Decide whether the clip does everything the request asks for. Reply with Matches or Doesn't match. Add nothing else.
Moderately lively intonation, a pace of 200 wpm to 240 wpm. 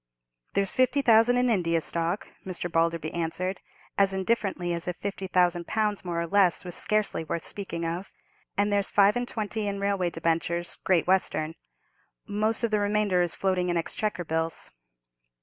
Doesn't match